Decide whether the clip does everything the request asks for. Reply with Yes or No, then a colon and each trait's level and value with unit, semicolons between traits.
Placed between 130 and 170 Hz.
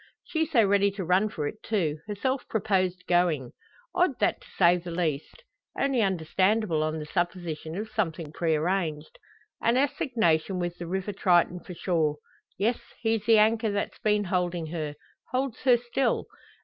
No: medium, 185 Hz